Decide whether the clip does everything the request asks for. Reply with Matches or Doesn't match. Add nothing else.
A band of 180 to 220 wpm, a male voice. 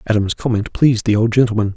Matches